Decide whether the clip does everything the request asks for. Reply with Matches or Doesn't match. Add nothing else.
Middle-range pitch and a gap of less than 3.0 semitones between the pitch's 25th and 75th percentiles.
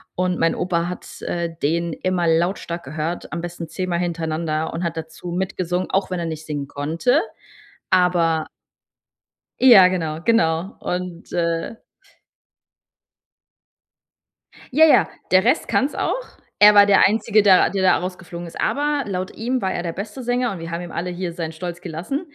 Matches